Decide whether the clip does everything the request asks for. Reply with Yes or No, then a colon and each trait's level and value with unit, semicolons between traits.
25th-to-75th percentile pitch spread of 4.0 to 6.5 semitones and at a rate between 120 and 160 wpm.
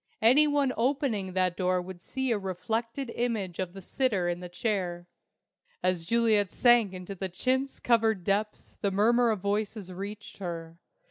Yes: average, 4.3 semitones; average, 155 wpm